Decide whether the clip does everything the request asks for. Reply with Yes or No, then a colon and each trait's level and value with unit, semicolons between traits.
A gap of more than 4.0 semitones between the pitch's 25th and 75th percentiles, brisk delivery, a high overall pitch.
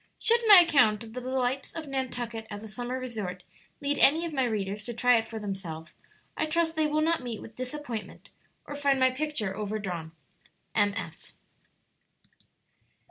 No: wide, 5.4 semitones; average, 165 wpm; high, 245 Hz